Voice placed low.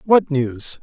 No: medium, 145 Hz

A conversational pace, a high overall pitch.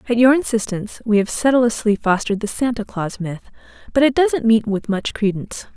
Yes: average, 190 wpm; high, 225 Hz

